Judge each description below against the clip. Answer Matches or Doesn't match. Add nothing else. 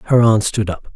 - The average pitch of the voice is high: Doesn't match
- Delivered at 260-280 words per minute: Doesn't match